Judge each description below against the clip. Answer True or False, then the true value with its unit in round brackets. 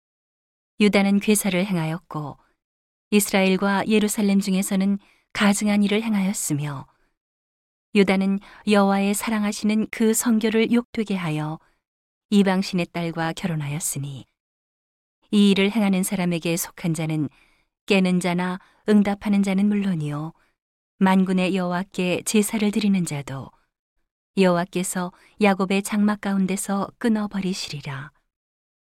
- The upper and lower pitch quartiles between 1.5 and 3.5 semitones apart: True (2.8 semitones)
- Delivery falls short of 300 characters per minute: True (270 characters per minute)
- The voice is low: False (195 Hz)